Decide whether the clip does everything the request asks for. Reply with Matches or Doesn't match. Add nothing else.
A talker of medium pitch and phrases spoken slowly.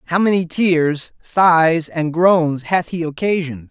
Doesn't match